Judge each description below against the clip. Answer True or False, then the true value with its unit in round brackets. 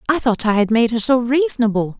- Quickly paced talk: True (240 wpm)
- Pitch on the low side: False (230 Hz)